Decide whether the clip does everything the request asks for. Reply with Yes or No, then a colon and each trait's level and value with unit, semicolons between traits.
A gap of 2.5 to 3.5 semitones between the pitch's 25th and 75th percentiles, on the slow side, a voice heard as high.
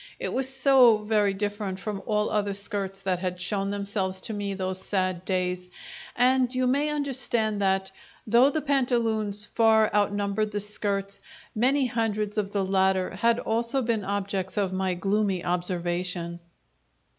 No: average, 3.0 semitones; average, 150 wpm; high, 205 Hz